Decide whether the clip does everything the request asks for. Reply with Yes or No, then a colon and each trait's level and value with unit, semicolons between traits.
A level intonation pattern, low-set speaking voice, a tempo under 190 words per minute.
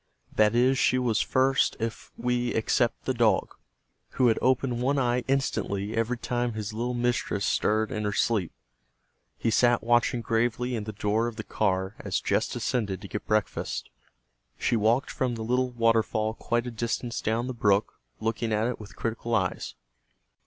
Yes: narrow, 2.1 semitones; low, 115 Hz; average, 175 wpm